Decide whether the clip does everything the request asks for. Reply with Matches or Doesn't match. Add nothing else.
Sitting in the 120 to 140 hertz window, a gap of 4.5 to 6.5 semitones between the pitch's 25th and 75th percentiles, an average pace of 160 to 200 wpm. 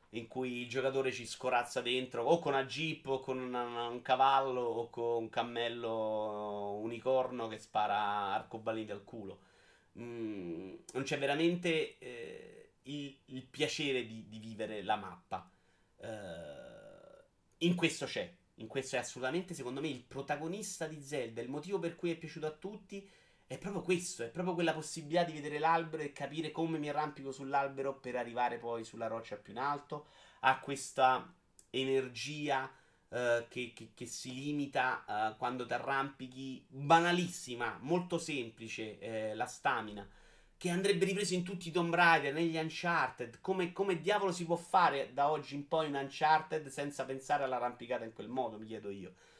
Matches